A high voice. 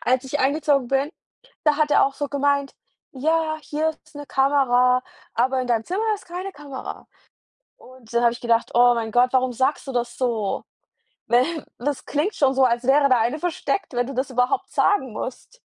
Yes: very high, 265 Hz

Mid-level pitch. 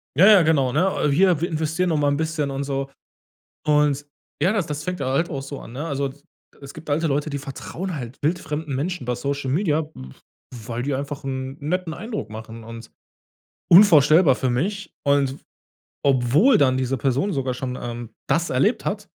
Yes: medium, 145 Hz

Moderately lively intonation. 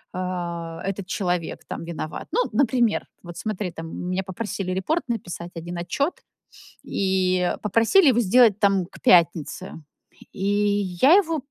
Yes: average, 4.0 semitones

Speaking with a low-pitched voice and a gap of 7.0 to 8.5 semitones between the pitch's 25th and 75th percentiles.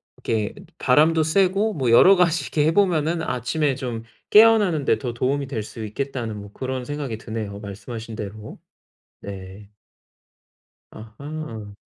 No: low, 130 Hz; wide, 6.2 semitones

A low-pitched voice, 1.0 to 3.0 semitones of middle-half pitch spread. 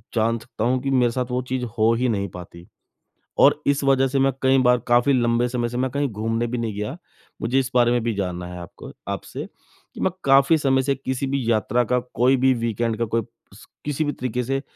Yes: low, 125 Hz; average, 2.7 semitones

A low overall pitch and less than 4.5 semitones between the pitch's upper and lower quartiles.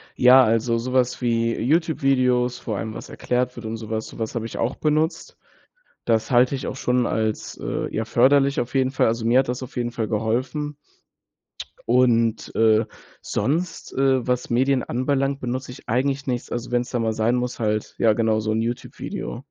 Yes: low, 125 Hz; narrow, 2.4 semitones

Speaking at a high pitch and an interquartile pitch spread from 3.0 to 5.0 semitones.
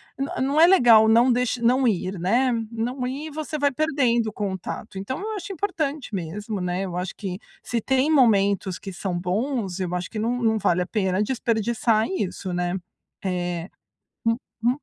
No: high, 225 Hz; wide, 5.4 semitones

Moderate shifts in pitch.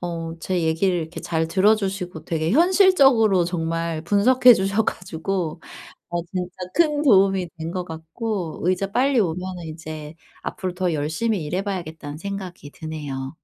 Yes: average, 3.6 semitones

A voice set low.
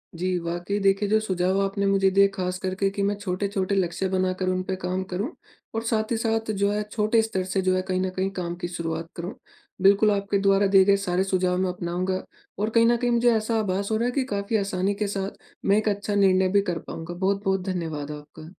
No: high, 195 Hz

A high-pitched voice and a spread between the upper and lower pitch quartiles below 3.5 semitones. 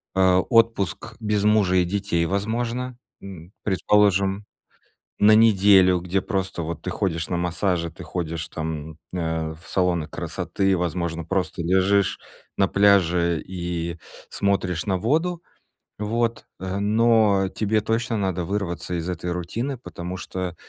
No: very low, 95 Hz; average, 3.1 semitones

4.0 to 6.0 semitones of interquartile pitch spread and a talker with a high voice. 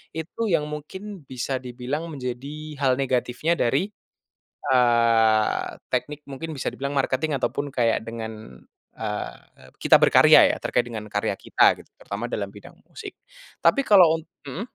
No: average, 4.8 semitones; low, 130 Hz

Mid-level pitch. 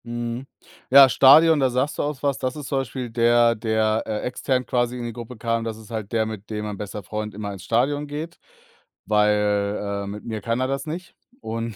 No: low, 115 Hz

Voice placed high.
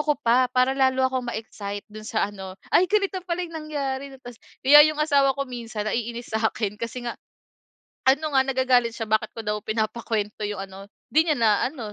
Yes: high, 245 Hz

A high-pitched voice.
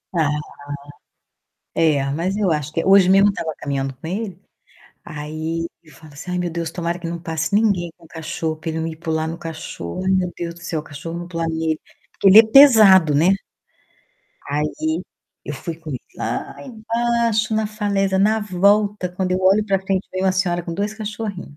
No: medium, 175 Hz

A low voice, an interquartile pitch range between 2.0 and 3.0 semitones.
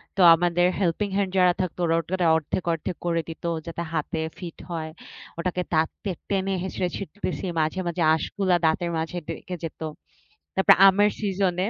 No: medium, 175 Hz; narrow, 2.4 semitones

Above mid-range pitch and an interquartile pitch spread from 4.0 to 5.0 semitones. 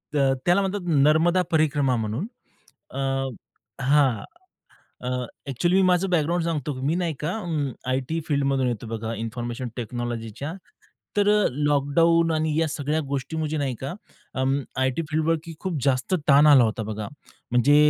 No: medium, 145 Hz; average, 4.3 semitones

